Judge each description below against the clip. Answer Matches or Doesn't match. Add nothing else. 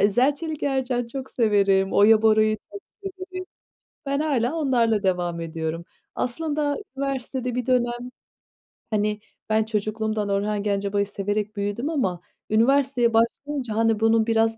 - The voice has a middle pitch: Doesn't match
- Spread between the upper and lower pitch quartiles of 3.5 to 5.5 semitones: Matches